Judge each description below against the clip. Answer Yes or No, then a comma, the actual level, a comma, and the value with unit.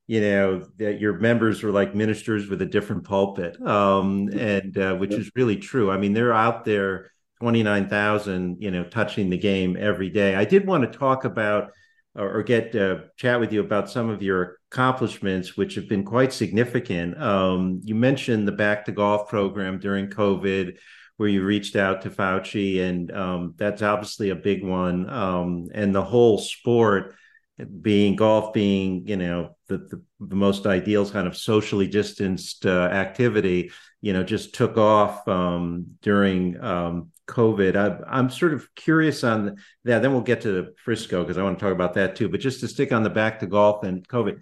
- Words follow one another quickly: No, average, 185 wpm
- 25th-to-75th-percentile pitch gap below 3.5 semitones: Yes, narrow, 2.5 semitones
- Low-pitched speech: Yes, low, 100 Hz